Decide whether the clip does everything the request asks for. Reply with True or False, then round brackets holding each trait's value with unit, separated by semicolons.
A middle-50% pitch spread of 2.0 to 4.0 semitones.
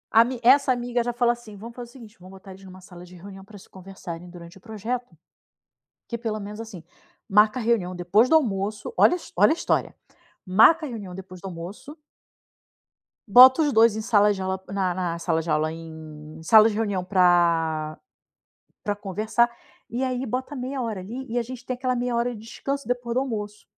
False (4.7 semitones)